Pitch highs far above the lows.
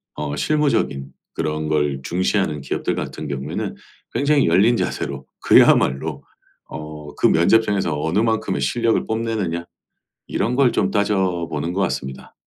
Yes: wide, 6.9 semitones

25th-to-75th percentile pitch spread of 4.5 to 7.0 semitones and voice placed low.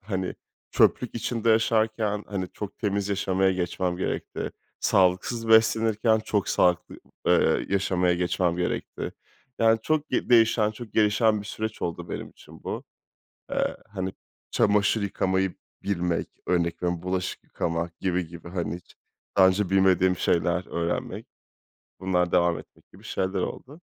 No: average, 3.3 semitones; very low, 95 Hz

